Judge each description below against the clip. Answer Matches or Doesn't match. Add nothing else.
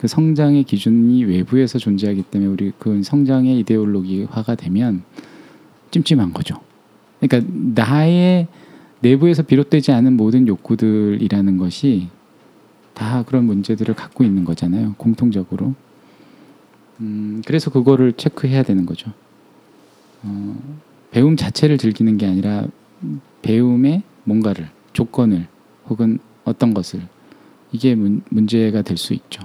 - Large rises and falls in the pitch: Doesn't match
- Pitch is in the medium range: Doesn't match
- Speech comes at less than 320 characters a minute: Matches